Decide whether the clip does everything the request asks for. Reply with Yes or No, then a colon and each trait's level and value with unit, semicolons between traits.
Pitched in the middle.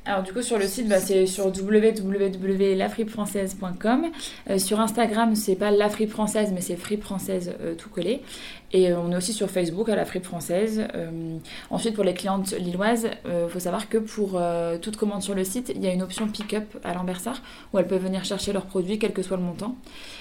No: high, 200 Hz